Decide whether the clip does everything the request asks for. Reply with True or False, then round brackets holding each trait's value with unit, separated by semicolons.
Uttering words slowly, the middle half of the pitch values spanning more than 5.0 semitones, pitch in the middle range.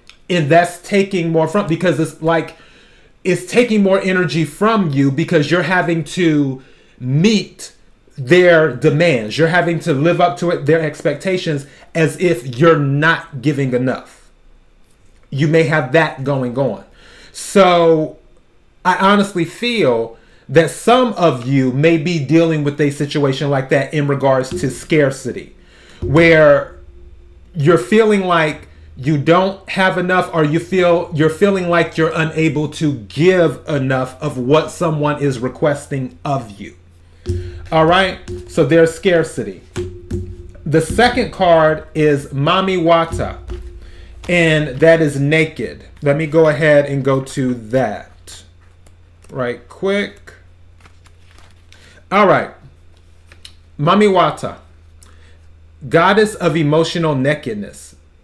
True (125 wpm; 5.6 semitones; 155 Hz)